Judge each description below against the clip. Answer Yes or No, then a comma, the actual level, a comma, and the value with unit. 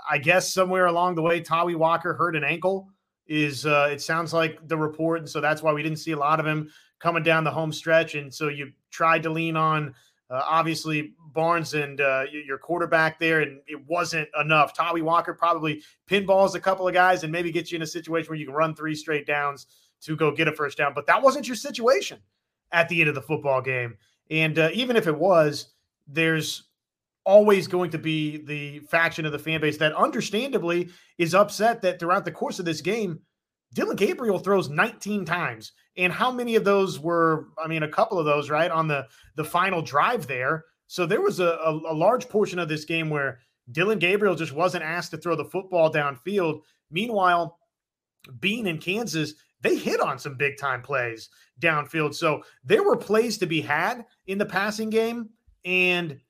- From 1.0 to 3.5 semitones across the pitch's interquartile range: Yes, average, 3.1 semitones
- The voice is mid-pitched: Yes, medium, 165 Hz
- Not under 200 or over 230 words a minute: Yes, fast, 205 wpm